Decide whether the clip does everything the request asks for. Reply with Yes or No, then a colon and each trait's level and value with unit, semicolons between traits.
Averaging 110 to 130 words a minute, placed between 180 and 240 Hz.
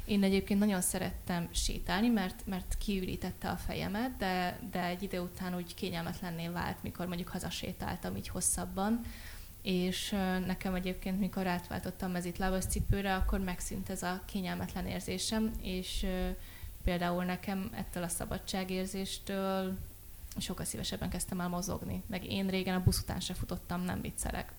No: average, 145 wpm; medium, 185 Hz